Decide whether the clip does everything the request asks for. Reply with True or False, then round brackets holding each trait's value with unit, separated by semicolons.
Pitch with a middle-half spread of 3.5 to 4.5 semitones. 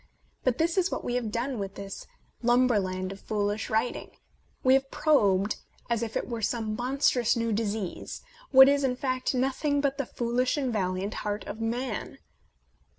True (3.9 semitones)